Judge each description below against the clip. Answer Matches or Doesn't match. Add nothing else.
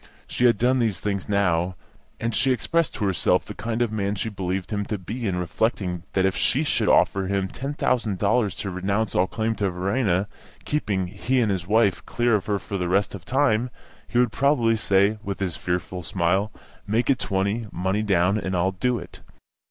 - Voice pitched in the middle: Doesn't match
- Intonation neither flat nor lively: Matches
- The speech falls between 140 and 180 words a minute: Doesn't match